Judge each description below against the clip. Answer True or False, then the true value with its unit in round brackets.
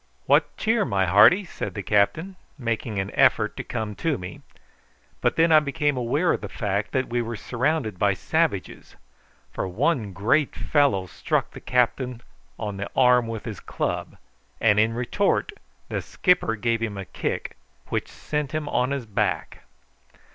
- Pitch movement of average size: False (5.9 semitones)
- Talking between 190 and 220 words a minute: False (165 wpm)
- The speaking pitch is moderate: False (120 Hz)